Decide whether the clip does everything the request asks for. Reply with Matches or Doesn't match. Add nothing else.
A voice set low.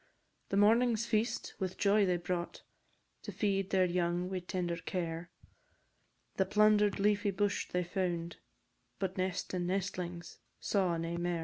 Doesn't match